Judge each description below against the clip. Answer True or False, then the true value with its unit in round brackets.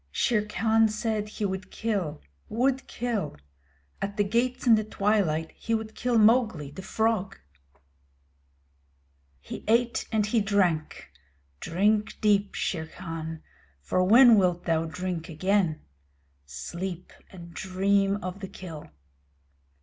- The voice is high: True (200 Hz)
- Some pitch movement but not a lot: True (4.1 semitones)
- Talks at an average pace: False (125 wpm)